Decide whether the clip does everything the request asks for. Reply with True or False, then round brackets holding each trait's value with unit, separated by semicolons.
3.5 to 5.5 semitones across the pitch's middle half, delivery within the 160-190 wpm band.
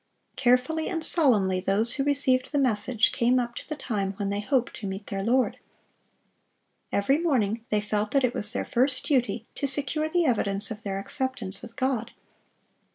True (4.7 semitones; 180 wpm)